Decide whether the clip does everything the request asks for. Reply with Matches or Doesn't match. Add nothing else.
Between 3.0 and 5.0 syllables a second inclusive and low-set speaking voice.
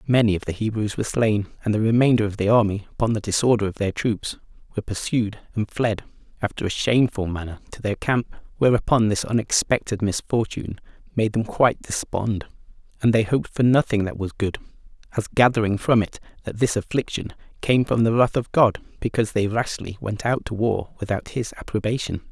Doesn't match